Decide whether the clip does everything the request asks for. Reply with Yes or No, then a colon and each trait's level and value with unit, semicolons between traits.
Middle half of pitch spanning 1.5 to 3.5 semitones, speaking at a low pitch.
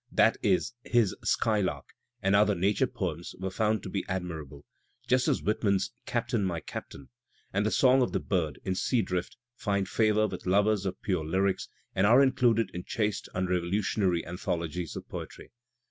Yes: average, 3.2 semitones; low, 100 Hz